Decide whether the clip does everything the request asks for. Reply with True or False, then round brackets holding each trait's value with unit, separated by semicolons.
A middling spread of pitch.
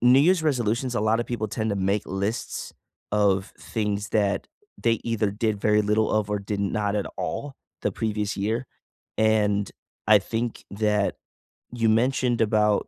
False (2.1 semitones)